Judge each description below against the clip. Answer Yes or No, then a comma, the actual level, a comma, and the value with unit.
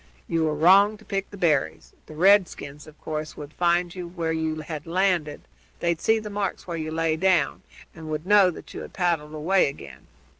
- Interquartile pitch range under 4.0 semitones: Yes, average, 3.4 semitones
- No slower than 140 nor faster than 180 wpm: No, average, 195 wpm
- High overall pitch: No, medium, 165 Hz